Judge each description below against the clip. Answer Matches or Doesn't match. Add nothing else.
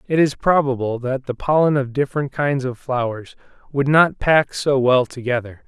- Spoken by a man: Matches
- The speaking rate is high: Doesn't match